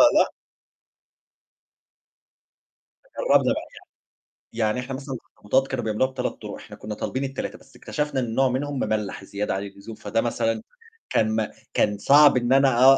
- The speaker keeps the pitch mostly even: No, average, 3.8 semitones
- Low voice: Yes, low, 125 Hz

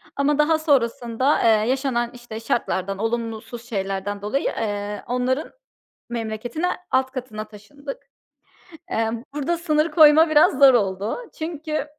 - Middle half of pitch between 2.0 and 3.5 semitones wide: No, average, 5.0 semitones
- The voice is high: Yes, high, 240 Hz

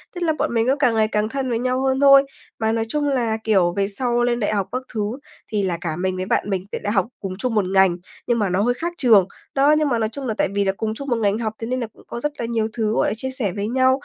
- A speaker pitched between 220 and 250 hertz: Yes, high, 225 Hz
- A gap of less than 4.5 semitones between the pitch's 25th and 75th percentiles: Yes, average, 3.9 semitones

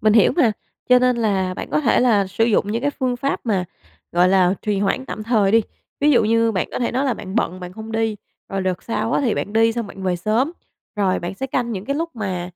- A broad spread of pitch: No, average, 4.0 semitones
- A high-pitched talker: Yes, high, 220 Hz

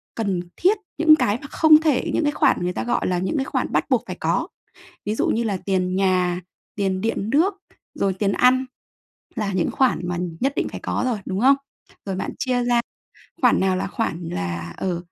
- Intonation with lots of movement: Yes, wide, 5.9 semitones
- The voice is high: Yes, high, 200 Hz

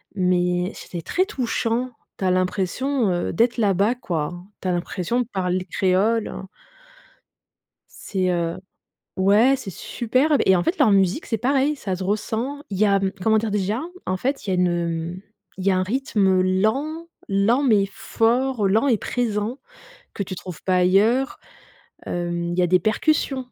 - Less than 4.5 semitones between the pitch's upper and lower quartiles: No, average, 5.0 semitones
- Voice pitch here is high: Yes, high, 205 Hz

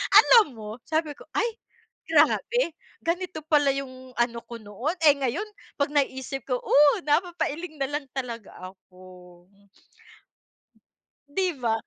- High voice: Yes, very high, 275 Hz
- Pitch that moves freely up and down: No, average, 5.0 semitones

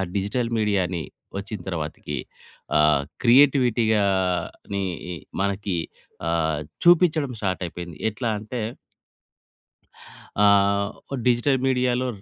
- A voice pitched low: Yes, low, 100 Hz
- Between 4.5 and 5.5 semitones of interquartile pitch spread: Yes, average, 4.8 semitones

